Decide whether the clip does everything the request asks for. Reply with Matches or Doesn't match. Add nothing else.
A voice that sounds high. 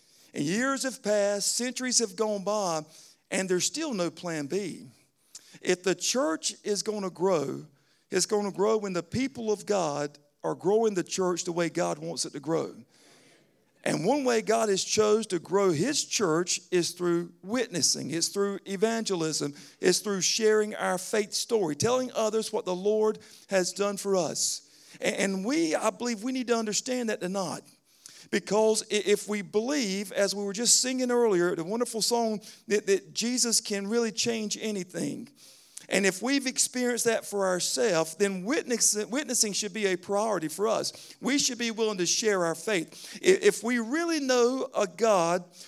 Matches